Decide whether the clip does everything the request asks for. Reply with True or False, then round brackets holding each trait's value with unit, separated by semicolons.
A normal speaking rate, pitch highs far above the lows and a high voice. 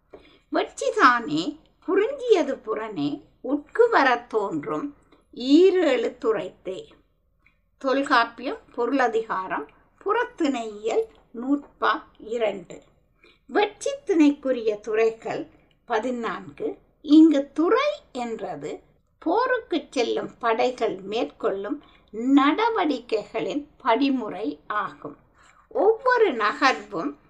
False (60 wpm; 7.4 semitones; 275 Hz)